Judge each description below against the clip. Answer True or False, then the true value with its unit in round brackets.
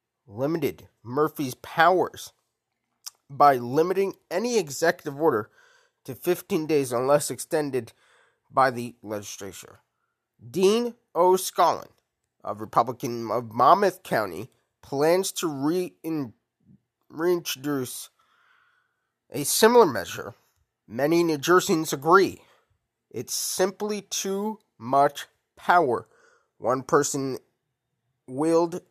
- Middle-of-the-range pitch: True (160 Hz)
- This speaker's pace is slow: True (85 wpm)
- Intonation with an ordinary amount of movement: False (6.6 semitones)